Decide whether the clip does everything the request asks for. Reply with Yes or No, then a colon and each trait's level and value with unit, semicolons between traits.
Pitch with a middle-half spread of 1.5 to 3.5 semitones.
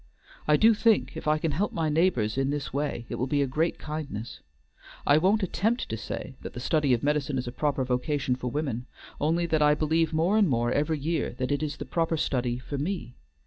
No: average, 4.0 semitones